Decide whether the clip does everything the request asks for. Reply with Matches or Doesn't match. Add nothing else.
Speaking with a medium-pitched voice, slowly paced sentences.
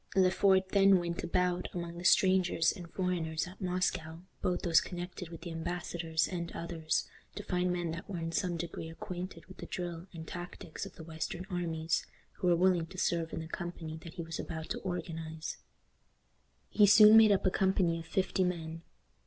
Doesn't match